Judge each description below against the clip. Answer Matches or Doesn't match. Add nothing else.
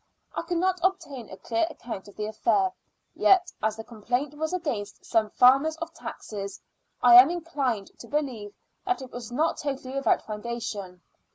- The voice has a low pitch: Doesn't match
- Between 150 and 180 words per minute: Matches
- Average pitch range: Doesn't match